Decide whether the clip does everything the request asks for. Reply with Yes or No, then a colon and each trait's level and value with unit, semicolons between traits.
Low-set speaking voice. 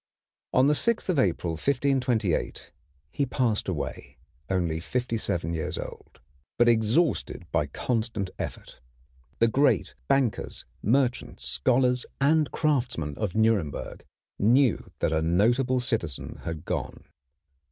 Yes: low, 115 Hz